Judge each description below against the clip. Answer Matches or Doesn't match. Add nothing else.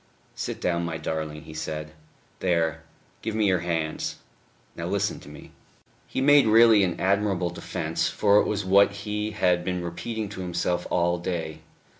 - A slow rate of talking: Doesn't match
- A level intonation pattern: Doesn't match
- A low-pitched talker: Matches